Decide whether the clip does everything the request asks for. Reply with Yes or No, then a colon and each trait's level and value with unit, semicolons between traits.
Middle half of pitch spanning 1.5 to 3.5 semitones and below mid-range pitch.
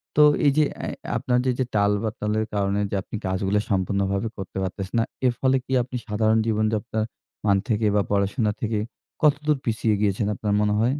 Yes: narrow, 2.5 semitones; low, 105 Hz